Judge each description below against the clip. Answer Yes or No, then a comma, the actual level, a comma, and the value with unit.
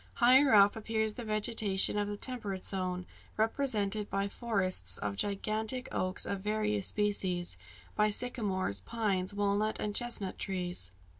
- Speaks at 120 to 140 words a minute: Yes, slow, 135 wpm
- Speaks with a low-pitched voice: No, high, 205 Hz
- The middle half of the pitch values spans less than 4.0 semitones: Yes, narrow, 2.4 semitones